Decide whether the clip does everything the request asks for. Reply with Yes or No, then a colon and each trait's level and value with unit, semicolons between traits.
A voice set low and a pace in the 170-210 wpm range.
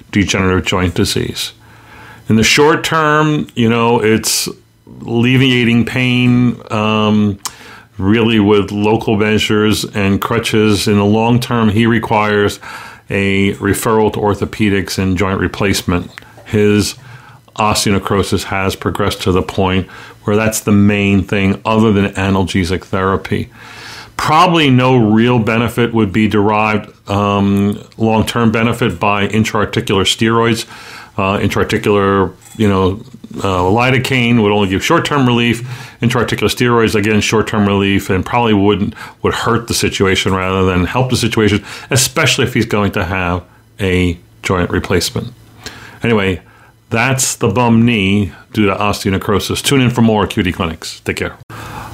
No: low, 110 Hz; slow, 135 wpm